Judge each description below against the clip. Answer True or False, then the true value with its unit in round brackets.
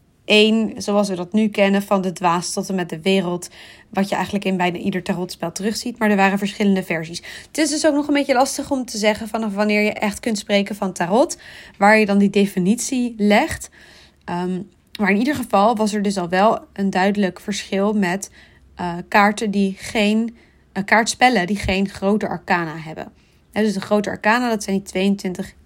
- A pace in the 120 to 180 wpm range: False (200 wpm)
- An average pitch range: False (2.1 semitones)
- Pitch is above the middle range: True (200 Hz)